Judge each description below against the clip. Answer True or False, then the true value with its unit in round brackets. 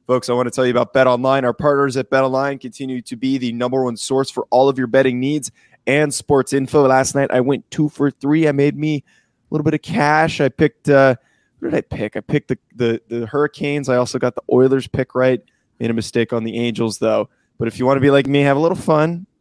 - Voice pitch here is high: False (135 Hz)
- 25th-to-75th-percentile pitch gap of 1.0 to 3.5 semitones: True (2.4 semitones)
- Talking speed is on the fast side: True (260 wpm)